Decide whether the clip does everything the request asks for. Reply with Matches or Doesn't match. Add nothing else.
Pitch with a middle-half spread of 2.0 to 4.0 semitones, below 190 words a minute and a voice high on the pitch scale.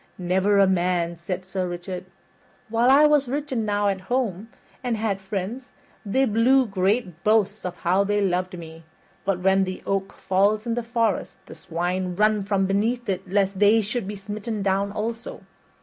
Matches